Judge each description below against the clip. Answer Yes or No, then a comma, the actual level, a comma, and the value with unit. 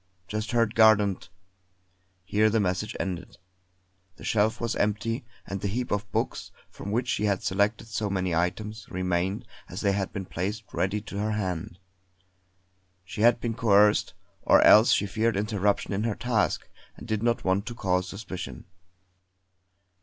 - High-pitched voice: No, low, 105 Hz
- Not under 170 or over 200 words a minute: No, average, 160 wpm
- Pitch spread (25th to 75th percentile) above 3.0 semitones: No, average, 2.7 semitones